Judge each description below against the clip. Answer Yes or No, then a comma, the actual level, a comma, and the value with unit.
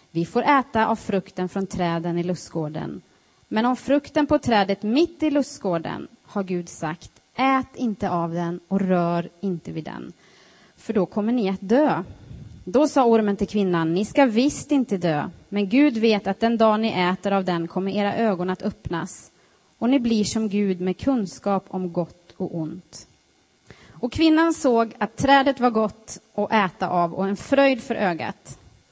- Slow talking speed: No, average, 180 wpm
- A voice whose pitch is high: Yes, high, 200 Hz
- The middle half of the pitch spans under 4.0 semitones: No, average, 5.1 semitones